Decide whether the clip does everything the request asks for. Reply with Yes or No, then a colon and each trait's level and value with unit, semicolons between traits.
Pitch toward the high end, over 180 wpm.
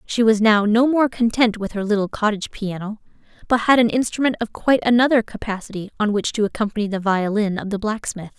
Yes: high, 220 Hz; average, 200 wpm